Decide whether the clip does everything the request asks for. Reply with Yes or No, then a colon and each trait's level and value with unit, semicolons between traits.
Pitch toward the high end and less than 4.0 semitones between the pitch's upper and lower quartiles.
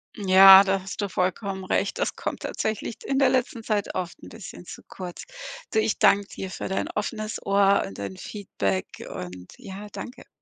Yes: high, 195 Hz; narrow, 2.6 semitones